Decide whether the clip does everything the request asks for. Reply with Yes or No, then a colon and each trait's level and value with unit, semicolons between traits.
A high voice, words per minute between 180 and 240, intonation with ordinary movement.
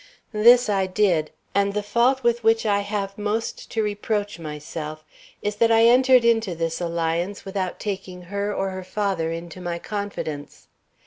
No: high, 200 Hz; average, 165 wpm; average, 3.9 semitones